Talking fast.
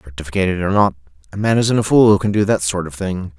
Yes: fast, 265 wpm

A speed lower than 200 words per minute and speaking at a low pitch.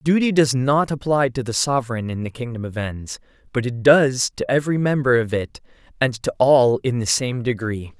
No: fast, 205 wpm; low, 125 Hz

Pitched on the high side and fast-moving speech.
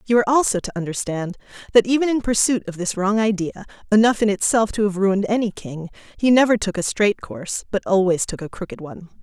Yes: high, 205 Hz; fast, 215 wpm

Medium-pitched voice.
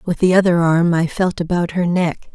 Yes: medium, 175 Hz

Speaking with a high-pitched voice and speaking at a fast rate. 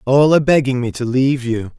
No: low, 130 Hz; fast, 235 wpm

